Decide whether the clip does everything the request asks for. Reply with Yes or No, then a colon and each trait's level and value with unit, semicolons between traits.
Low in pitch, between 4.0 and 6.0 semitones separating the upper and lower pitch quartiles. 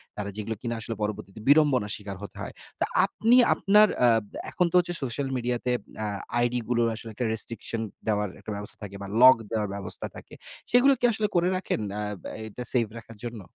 Yes: low, 115 Hz; average, 4.3 semitones